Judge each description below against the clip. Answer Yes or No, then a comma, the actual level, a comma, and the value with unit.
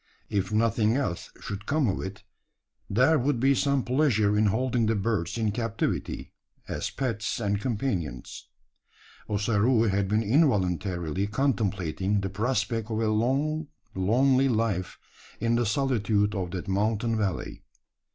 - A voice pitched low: Yes, low, 110 Hz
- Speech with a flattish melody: No, average, 3.8 semitones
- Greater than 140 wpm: No, slow, 135 wpm